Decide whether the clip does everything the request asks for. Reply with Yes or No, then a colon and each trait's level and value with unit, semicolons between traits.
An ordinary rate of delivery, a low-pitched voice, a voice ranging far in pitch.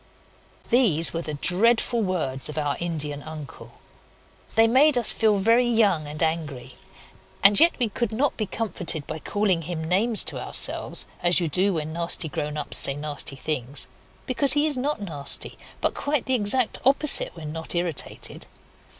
No: average, 165 wpm; medium, 180 Hz; wide, 7.0 semitones